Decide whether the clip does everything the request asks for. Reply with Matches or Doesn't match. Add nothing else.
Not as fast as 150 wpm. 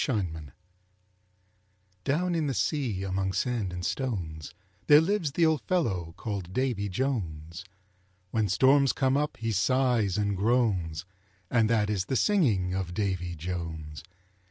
Matches